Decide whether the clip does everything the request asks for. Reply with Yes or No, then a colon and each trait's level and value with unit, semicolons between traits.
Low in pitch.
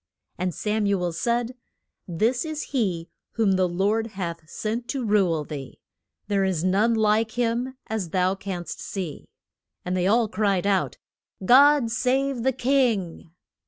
No: high, 210 Hz